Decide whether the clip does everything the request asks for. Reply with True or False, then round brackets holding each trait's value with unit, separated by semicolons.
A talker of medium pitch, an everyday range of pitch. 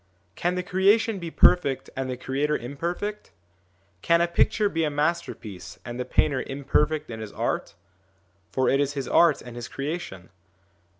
True (145 Hz; 4.8 semitones)